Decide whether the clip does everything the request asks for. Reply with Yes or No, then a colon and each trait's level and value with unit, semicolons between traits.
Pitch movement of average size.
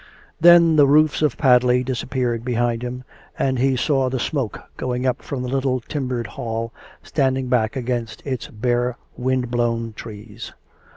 No: narrow, 2.0 semitones